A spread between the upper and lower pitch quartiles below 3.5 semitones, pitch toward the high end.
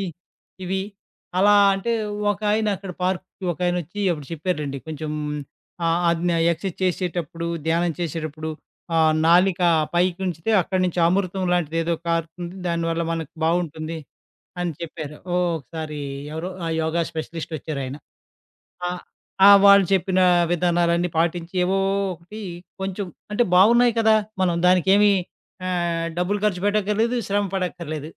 No: narrow, 2.6 semitones; medium, 175 Hz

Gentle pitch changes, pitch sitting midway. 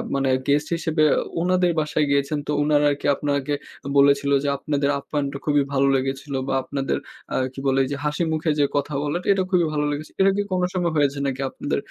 Yes: narrow, 1.9 semitones; medium, 145 Hz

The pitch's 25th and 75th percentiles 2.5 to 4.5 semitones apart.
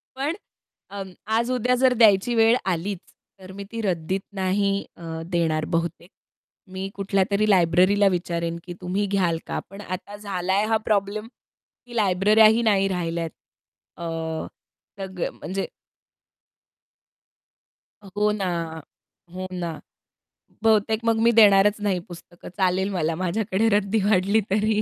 Yes: average, 2.8 semitones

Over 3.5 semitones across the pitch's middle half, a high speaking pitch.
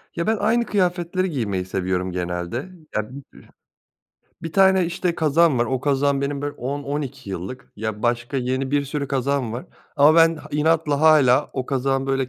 No: average, 4.5 semitones; medium, 140 Hz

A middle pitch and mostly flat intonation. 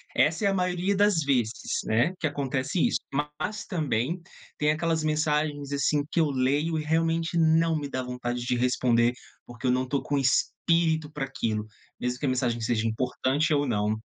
No: medium, 145 Hz; average, 4.4 semitones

